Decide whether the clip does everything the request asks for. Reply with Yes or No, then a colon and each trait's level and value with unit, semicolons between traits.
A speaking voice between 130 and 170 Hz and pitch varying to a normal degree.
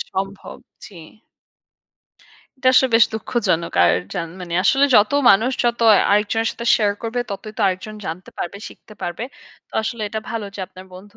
No: high, 210 Hz; average, 3.4 semitones